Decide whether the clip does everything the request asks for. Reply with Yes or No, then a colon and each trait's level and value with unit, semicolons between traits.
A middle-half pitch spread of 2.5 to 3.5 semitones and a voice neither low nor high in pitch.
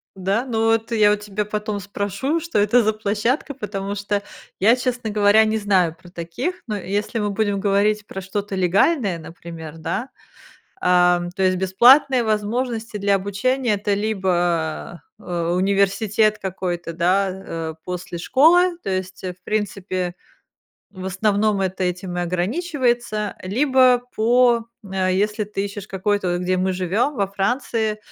No: average, 3.0 semitones; high, 200 Hz